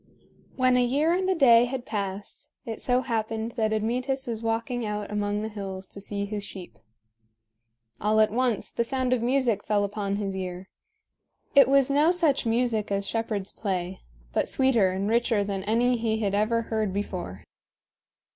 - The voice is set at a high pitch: Yes, high, 220 Hz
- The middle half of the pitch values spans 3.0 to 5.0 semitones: Yes, average, 3.5 semitones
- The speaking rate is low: No, average, 175 wpm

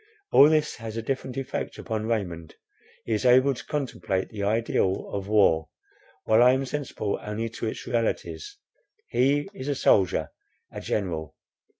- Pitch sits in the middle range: No, low, 115 Hz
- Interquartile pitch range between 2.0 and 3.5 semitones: No, average, 4.6 semitones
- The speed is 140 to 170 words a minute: Yes, average, 160 wpm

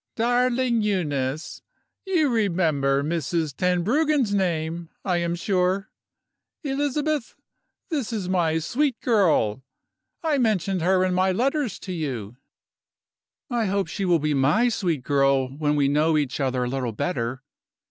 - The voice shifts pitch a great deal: Yes, wide, 7.5 semitones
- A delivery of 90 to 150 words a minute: Yes, slow, 135 wpm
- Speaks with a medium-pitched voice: Yes, medium, 180 Hz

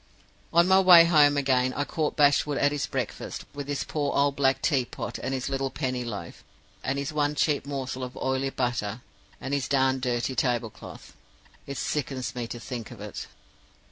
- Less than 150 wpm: No, average, 185 wpm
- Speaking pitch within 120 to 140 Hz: Yes, low, 135 Hz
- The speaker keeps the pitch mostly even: Yes, narrow, 2.2 semitones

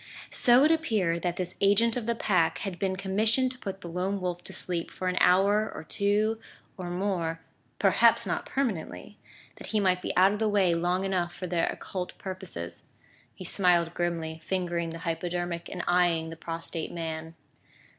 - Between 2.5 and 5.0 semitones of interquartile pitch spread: Yes, average, 2.9 semitones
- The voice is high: No, medium, 180 Hz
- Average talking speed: Yes, average, 180 wpm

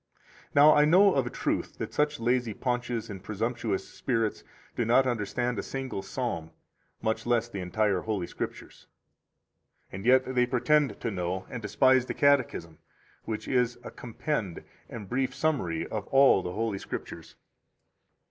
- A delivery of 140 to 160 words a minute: Yes, average, 155 wpm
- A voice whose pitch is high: No, low, 120 Hz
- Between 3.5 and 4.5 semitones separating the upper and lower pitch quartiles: Yes, average, 4.2 semitones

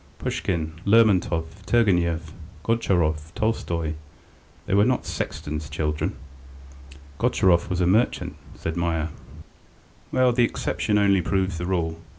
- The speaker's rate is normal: No, slow, 115 wpm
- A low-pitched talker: Yes, very low, 90 Hz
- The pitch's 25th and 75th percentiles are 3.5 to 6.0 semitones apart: Yes, average, 3.9 semitones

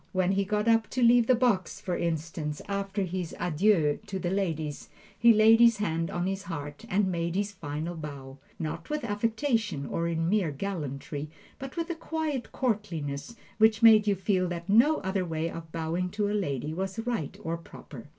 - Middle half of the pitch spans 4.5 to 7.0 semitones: Yes, average, 4.9 semitones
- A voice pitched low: No, high, 190 Hz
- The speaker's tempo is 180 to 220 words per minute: Yes, average, 190 wpm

